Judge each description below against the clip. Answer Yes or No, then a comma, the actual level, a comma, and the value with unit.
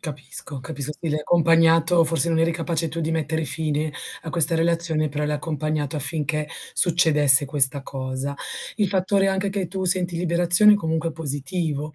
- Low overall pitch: No, medium, 160 Hz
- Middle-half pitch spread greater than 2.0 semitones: Yes, narrow, 2.4 semitones